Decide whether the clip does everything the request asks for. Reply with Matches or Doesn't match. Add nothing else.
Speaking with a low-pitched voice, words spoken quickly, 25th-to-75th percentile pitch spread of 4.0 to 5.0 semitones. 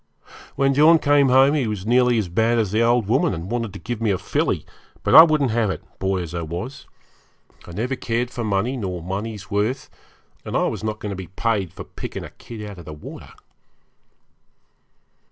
Matches